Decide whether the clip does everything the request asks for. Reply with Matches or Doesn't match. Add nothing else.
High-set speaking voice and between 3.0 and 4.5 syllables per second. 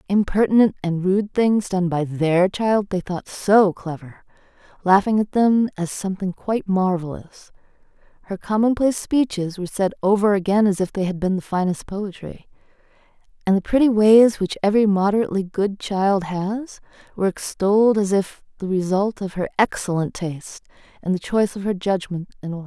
Doesn't match